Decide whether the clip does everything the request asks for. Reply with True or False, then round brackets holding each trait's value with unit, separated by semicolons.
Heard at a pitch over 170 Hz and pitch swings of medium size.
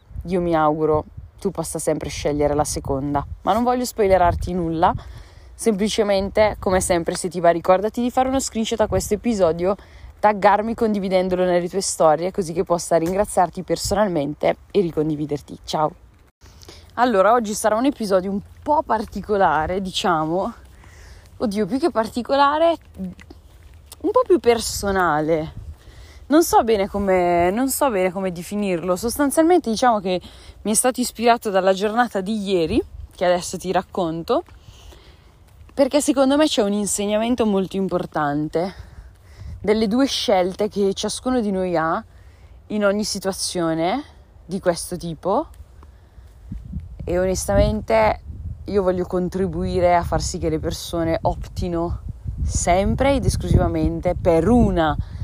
True (185 Hz; 4.7 semitones)